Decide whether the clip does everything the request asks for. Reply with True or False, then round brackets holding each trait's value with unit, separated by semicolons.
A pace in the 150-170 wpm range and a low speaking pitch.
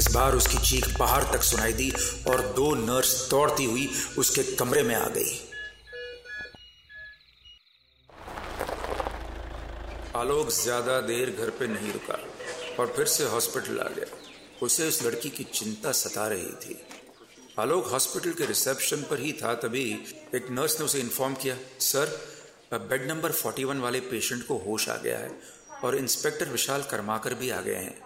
False (155 wpm; 160 Hz)